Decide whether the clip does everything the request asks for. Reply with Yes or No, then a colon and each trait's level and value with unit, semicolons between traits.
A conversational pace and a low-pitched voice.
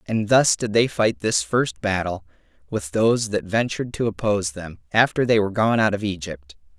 Yes: average, 195 wpm; low, 105 Hz